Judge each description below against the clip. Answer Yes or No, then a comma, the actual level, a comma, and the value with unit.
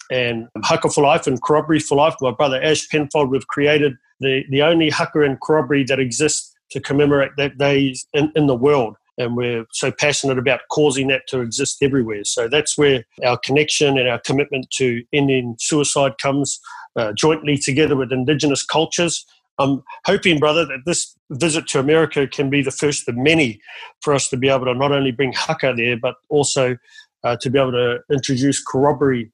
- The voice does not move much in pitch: Yes, narrow, 2.3 semitones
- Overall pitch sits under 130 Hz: No, medium, 140 Hz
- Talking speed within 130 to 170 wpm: No, average, 190 wpm